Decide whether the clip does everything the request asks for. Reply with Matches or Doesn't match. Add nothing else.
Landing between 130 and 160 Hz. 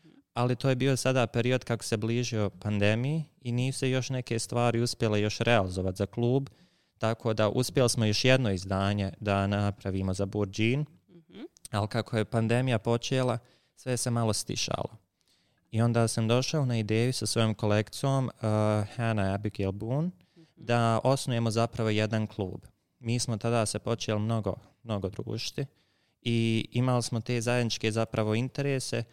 Doesn't match